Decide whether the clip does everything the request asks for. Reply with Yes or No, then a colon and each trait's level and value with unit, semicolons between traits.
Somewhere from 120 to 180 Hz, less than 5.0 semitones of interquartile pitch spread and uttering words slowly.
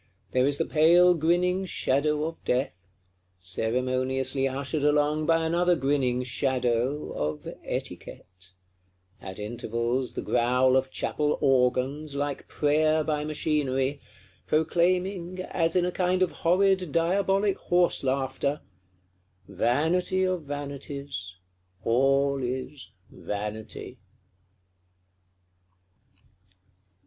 Yes: medium, 140 Hz; average, 4.4 semitones; slow, 100 wpm